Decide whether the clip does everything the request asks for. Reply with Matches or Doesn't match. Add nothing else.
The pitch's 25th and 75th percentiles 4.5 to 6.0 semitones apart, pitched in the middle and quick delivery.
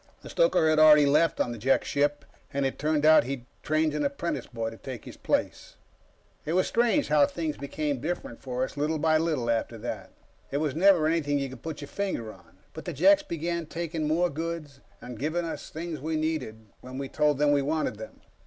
Doesn't match